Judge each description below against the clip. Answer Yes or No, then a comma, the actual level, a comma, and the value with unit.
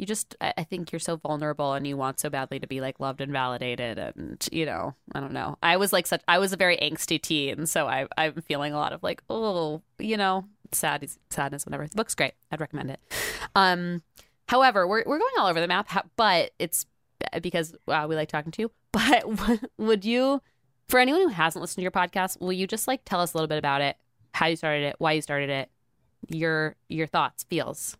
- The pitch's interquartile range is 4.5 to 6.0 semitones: Yes, average, 4.9 semitones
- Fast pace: Yes, fast, 225 wpm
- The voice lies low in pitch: No, medium, 160 Hz